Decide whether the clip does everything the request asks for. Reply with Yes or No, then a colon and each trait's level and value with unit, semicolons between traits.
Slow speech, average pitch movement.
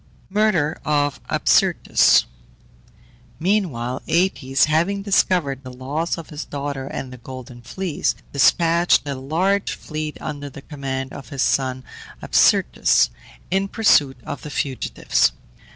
Yes: slow, 120 wpm; average, 4.3 semitones